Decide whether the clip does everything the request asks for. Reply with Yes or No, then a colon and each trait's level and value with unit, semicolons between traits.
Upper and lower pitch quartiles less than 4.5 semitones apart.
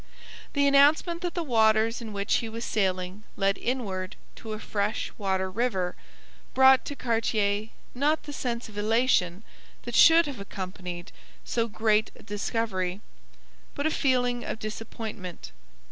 Yes: average, 4.1 semitones